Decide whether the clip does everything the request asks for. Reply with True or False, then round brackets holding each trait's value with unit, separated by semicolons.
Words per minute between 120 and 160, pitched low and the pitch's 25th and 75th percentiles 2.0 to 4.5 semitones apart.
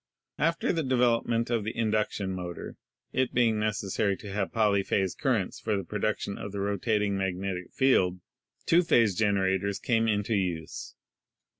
True (155 wpm; 105 Hz; 3.0 semitones)